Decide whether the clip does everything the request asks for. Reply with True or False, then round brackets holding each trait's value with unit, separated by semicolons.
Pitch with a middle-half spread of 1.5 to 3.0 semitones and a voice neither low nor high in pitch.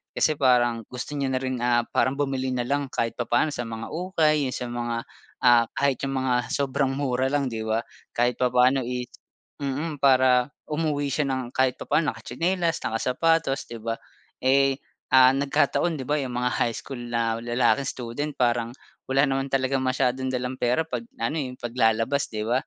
False (2.5 semitones; 130 Hz)